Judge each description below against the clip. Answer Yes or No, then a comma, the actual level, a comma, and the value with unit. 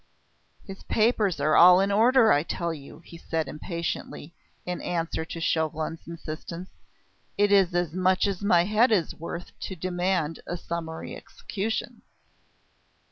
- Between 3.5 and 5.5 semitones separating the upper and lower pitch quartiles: No, average, 3.0 semitones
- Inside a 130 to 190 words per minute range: Yes, average, 140 wpm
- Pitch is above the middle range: No, medium, 175 Hz